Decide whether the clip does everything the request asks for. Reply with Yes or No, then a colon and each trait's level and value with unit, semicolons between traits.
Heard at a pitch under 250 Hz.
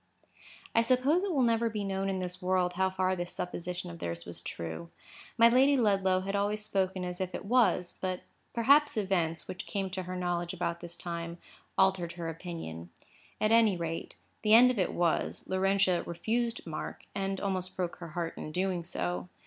Yes: medium, 185 Hz